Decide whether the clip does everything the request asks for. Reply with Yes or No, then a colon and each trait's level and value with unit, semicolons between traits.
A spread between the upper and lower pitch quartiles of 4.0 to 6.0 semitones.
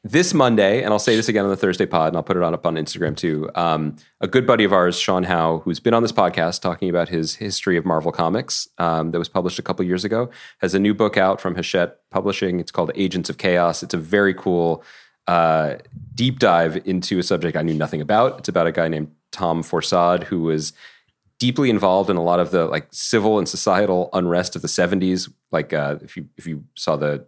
No: average, 3.1 semitones